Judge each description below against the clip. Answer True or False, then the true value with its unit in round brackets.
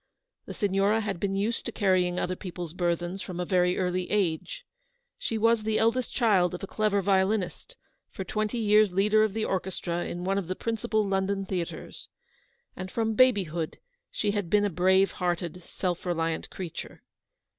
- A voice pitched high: True (195 Hz)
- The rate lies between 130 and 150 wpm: False (170 wpm)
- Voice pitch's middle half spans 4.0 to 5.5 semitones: False (3.0 semitones)